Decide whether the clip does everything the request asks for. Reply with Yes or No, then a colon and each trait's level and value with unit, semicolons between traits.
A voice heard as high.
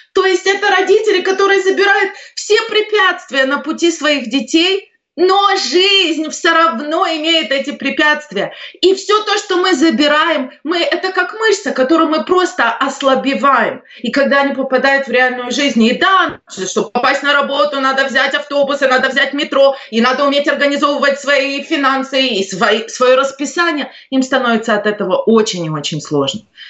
Yes: very high, 285 Hz